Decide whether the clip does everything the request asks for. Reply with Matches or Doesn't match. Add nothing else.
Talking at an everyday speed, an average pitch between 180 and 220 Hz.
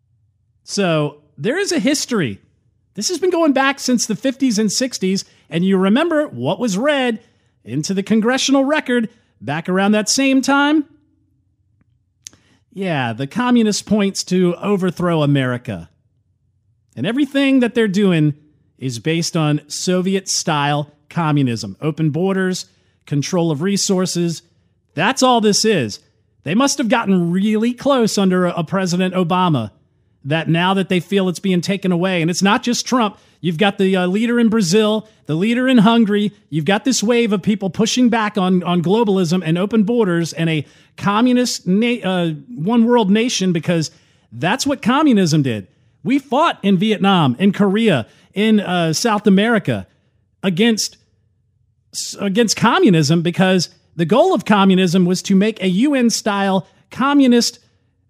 Matches